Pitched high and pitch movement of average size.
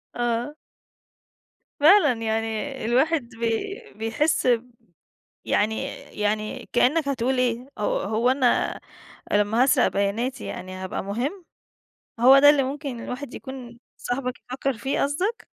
Yes: very high, 250 Hz; average, 3.7 semitones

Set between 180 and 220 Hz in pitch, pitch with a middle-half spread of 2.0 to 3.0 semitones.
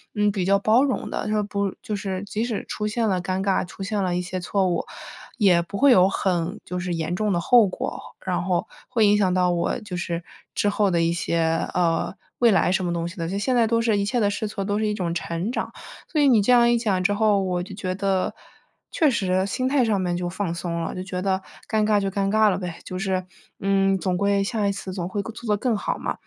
Yes: high, 195 Hz; average, 2.7 semitones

